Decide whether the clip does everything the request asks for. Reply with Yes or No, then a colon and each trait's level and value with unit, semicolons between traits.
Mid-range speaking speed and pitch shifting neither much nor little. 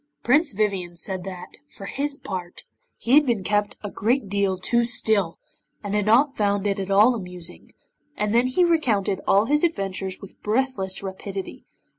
Yes: average, 170 wpm; average, 3.9 semitones